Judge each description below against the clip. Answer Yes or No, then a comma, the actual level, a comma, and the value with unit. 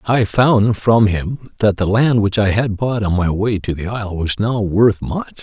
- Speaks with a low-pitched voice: Yes, low, 105 Hz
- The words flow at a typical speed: No, fast, 230 wpm